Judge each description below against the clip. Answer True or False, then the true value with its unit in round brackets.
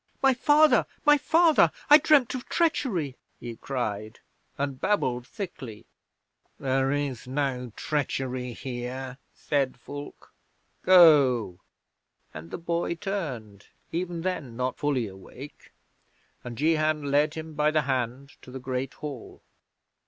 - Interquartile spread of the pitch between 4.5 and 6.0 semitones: True (5.0 semitones)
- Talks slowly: True (125 wpm)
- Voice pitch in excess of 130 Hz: True (140 Hz)